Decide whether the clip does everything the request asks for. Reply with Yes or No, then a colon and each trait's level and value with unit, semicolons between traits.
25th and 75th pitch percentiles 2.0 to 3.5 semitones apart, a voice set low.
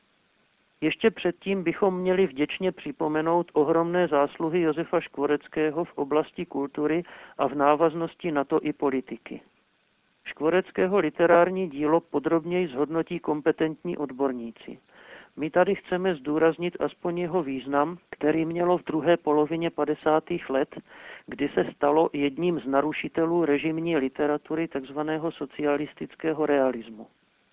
No: average, 2.8 semitones; medium, 155 Hz